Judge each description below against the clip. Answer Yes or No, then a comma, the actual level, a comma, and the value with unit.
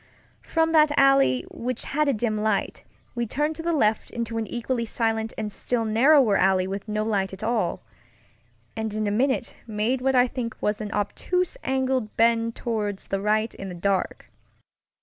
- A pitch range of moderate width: Yes, average, 3.6 semitones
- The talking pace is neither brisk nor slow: Yes, average, 180 wpm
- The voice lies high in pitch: Yes, high, 225 Hz